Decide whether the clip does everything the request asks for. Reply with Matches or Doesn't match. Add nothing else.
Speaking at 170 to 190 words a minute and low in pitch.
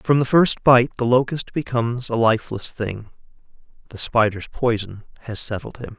Doesn't match